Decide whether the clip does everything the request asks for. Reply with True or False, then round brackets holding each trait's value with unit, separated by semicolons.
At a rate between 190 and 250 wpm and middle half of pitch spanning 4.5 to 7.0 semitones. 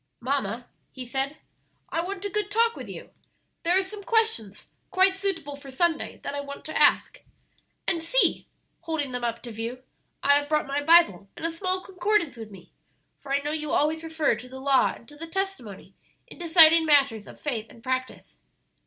True (195 wpm; 5.1 semitones)